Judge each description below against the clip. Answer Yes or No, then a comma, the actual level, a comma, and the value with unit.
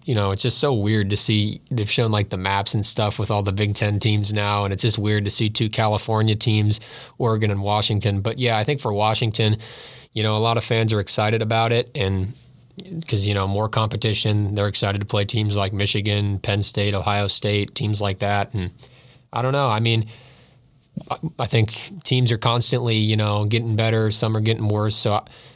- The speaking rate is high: Yes, fast, 215 wpm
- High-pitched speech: No, low, 110 Hz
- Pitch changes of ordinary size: No, narrow, 2.2 semitones